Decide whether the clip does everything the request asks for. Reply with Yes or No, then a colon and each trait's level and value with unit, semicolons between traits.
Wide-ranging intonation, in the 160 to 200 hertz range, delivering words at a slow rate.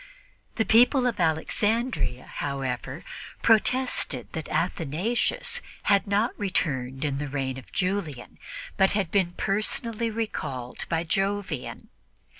Yes: wide, 7.5 semitones; medium, 185 Hz; slow, 110 wpm